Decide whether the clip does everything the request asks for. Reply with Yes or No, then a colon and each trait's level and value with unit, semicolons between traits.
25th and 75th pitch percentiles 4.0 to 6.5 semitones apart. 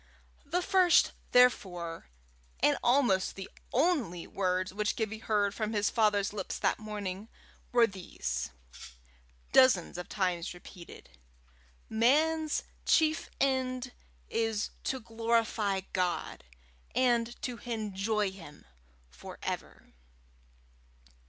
Yes: average, 4.6 semitones